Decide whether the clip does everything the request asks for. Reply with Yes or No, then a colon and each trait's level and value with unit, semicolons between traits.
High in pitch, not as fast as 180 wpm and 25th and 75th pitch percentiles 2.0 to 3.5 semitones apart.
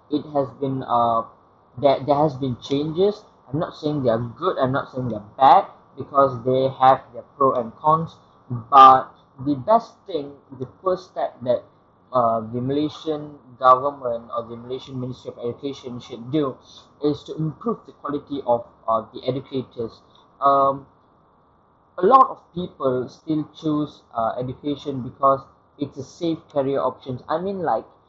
No: low, 135 Hz; average, 160 wpm; average, 2.9 semitones